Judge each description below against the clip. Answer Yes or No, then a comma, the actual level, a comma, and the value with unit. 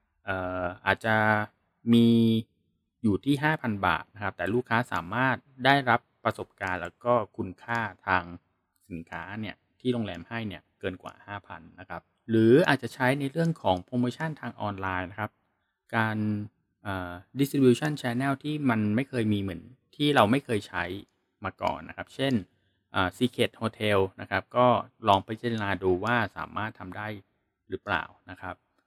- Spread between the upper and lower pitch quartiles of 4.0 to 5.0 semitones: Yes, average, 4.6 semitones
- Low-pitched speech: Yes, low, 110 Hz